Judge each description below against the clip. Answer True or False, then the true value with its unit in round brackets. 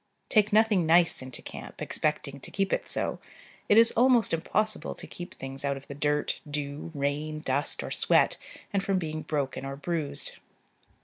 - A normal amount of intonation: False (5.7 semitones)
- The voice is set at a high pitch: False (155 Hz)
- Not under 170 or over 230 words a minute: True (175 wpm)